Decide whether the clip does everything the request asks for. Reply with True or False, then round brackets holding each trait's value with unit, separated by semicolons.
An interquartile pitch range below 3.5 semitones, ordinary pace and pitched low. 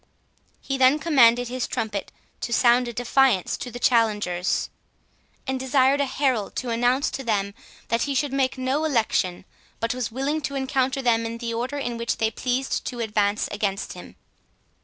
False (2.8 semitones; 175 wpm; 245 Hz)